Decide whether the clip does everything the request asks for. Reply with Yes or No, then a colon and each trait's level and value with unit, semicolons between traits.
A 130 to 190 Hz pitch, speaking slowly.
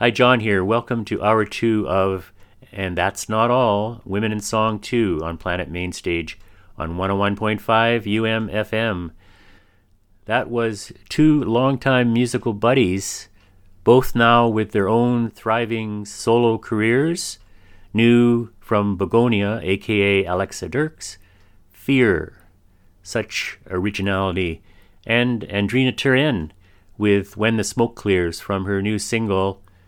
No: low, 105 Hz; slow, 115 wpm